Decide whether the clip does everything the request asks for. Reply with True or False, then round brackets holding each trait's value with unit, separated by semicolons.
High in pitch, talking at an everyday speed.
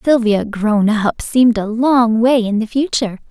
True (230 Hz; 180 wpm)